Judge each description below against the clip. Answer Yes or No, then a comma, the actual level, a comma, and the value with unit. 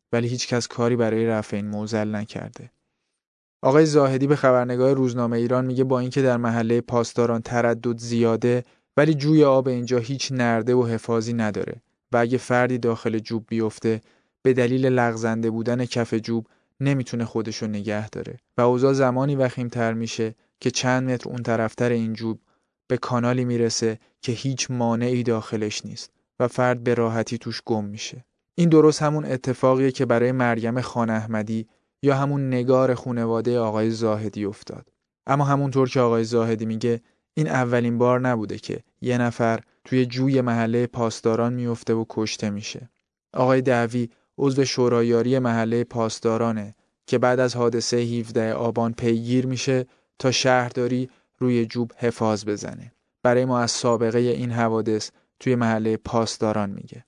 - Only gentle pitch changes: Yes, narrow, 1.9 semitones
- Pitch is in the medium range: No, low, 120 Hz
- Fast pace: Yes, fast, 150 wpm